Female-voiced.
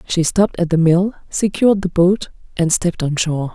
Yes: female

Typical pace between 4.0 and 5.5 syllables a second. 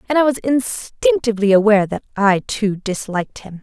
Yes: 5.4 syllables/s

